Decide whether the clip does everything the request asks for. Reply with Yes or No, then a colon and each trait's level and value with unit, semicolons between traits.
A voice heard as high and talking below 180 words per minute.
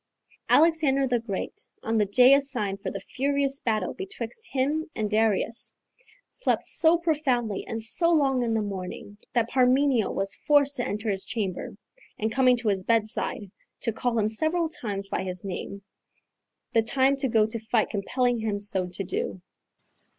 Yes: high, 230 Hz; average, 165 wpm